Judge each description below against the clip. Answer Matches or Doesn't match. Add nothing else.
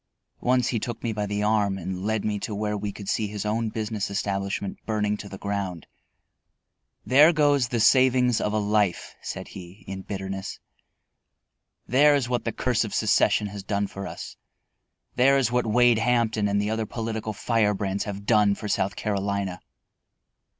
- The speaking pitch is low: Matches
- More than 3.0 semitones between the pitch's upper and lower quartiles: Doesn't match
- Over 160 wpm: Matches